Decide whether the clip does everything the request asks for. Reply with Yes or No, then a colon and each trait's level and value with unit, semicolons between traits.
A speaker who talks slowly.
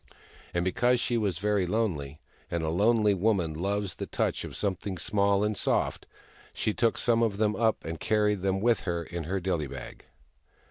No: average, 185 wpm